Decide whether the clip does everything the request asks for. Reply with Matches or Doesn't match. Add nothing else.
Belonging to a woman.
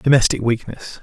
Doesn't match